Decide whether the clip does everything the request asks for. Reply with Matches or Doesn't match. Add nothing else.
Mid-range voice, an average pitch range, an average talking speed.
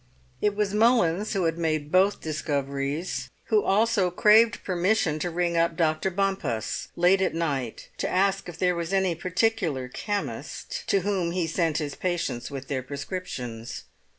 Matches